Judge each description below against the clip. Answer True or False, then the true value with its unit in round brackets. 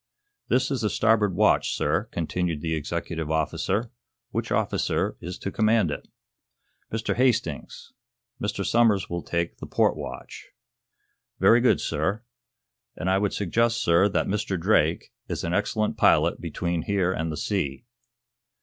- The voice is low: True (95 Hz)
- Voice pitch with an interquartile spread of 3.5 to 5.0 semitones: True (4.4 semitones)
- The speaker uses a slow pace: False (145 wpm)